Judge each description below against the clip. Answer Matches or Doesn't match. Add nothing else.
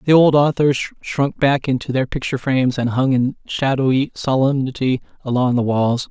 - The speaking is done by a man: Matches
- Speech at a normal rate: Matches